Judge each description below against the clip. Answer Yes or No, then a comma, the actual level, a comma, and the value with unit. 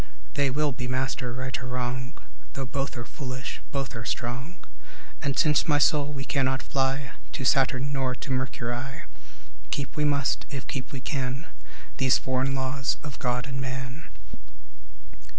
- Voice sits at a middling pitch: No, low, 130 Hz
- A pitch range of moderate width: No, narrow, 1.5 semitones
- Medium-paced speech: Yes, average, 155 wpm